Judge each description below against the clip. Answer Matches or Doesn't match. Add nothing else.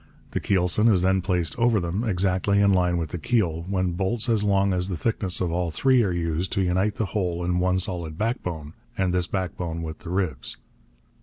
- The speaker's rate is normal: Doesn't match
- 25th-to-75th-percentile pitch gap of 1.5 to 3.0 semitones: Matches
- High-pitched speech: Doesn't match